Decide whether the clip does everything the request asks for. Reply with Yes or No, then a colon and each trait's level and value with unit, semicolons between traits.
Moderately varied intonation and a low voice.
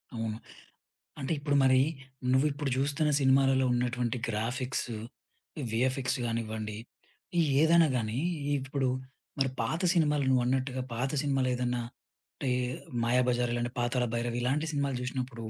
No: narrow, 2.2 semitones; low, 130 Hz